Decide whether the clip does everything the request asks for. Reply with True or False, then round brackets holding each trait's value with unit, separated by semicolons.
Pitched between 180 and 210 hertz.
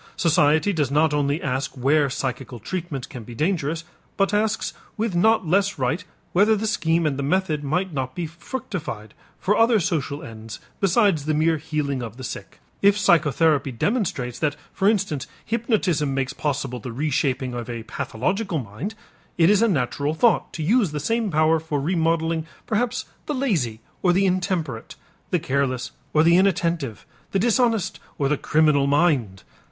False (155 Hz)